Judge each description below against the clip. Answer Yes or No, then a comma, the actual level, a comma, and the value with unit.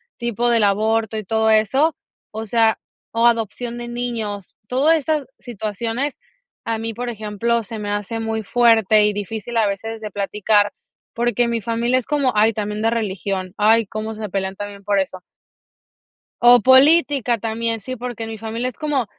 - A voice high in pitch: Yes, high, 225 Hz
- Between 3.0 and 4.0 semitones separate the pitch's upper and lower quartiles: No, narrow, 2.4 semitones